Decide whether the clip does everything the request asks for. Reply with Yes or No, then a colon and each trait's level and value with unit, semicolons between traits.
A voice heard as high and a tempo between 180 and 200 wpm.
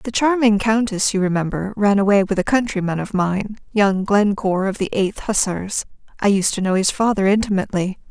Yes: high, 200 Hz; average, 185 wpm